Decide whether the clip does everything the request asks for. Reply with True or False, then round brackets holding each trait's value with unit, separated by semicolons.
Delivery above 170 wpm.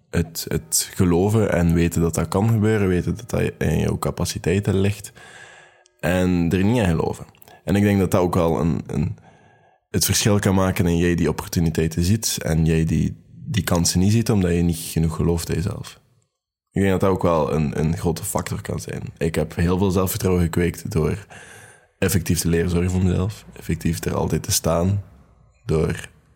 True (190 wpm)